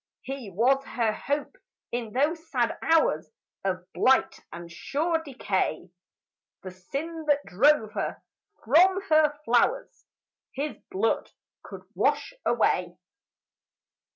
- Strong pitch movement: Yes, wide, 6.3 semitones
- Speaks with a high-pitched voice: Yes, very high, 270 Hz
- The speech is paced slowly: Yes, slow, 110 wpm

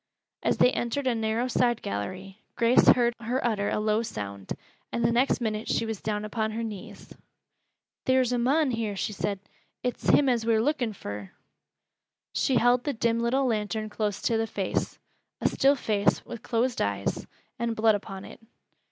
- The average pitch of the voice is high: Yes, high, 225 Hz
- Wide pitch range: No, narrow, 2.5 semitones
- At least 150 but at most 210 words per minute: Yes, average, 180 wpm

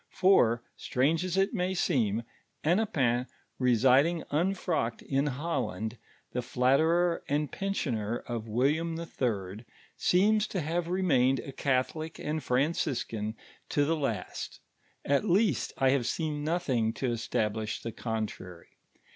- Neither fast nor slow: No, slow, 125 wpm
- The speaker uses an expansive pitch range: Yes, wide, 6.0 semitones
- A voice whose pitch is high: No, medium, 140 Hz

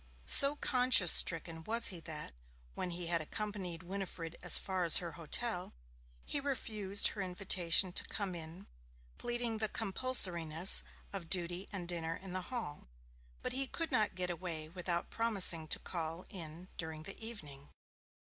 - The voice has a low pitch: No, medium, 180 Hz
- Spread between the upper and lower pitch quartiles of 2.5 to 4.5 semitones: Yes, average, 4.0 semitones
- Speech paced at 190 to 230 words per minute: No, average, 150 wpm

